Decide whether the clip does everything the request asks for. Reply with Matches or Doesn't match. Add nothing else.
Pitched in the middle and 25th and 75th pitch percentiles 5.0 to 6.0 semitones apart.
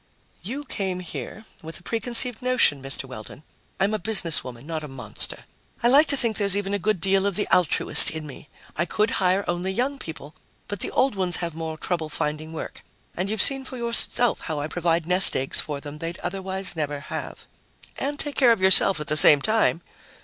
Matches